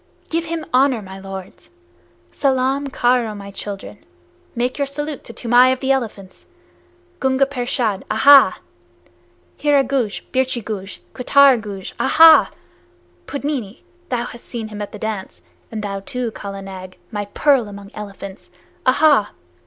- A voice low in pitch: No, high, 240 Hz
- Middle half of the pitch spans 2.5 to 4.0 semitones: No, average, 5.1 semitones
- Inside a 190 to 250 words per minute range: No, slow, 135 wpm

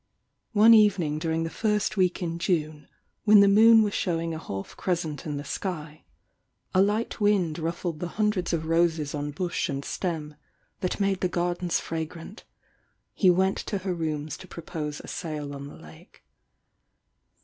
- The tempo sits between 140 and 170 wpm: Yes, average, 165 wpm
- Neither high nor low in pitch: Yes, medium, 170 Hz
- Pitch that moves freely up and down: No, average, 3.8 semitones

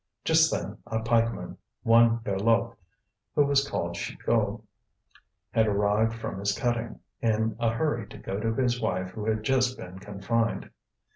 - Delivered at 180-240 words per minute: No, average, 150 wpm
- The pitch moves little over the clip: Yes, narrow, 2.2 semitones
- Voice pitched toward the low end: Yes, low, 115 Hz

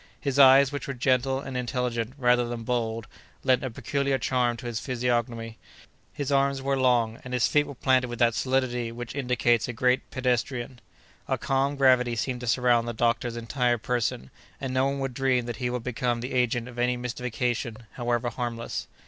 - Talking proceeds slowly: No, average, 190 wpm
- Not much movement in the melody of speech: Yes, narrow, 1.7 semitones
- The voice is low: Yes, low, 125 Hz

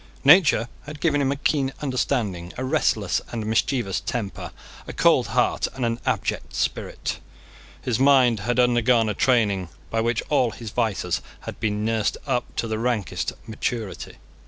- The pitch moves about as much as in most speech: Yes, average, 3.4 semitones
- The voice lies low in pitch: Yes, low, 120 Hz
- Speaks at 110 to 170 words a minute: Yes, average, 160 wpm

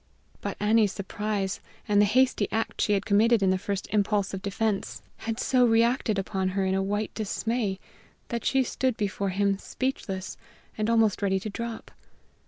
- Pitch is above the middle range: Yes, high, 210 Hz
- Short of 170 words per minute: No, average, 175 wpm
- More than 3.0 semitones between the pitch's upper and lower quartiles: No, narrow, 2.5 semitones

